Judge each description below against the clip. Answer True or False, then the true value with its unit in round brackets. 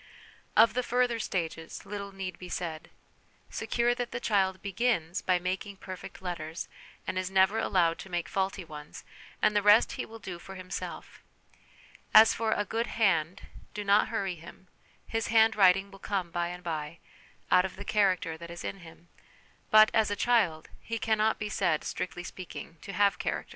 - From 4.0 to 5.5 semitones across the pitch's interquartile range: False (3.6 semitones)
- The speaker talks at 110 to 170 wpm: False (180 wpm)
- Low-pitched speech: False (190 Hz)